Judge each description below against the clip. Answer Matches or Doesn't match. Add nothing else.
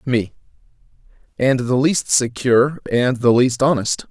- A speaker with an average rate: Doesn't match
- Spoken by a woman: Doesn't match